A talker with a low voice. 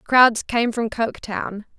No: high, 225 Hz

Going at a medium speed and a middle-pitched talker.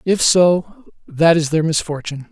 Yes: average, 155 wpm; medium, 165 Hz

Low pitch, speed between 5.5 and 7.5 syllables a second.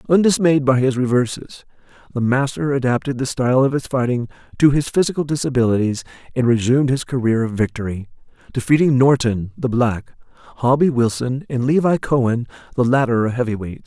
Yes: low, 130 Hz; 5.9 syllables/s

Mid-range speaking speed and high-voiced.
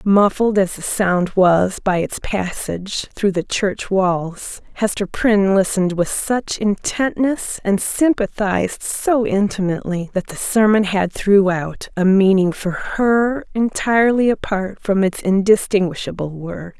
No: slow, 130 wpm; high, 195 Hz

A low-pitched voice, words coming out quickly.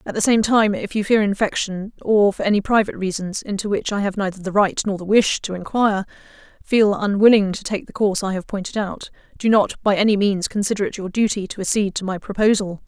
No: high, 200 Hz; fast, 230 wpm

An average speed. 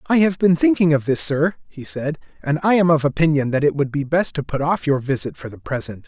No: fast, 265 wpm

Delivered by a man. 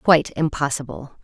No: female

